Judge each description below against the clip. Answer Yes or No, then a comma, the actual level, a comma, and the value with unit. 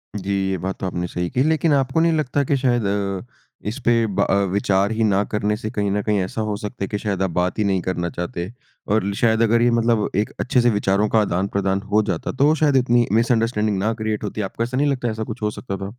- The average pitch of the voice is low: Yes, low, 105 Hz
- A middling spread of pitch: Yes, average, 3.5 semitones